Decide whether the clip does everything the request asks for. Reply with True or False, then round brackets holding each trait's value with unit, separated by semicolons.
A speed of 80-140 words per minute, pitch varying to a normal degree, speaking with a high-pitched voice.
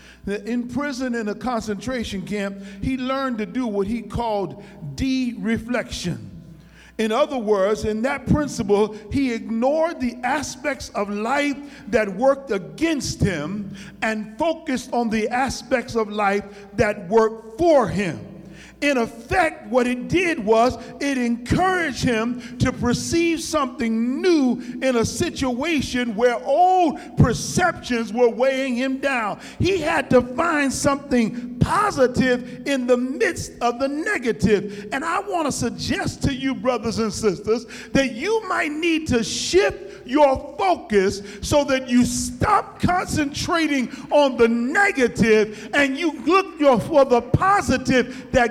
True (135 wpm; 4.0 semitones; 245 Hz)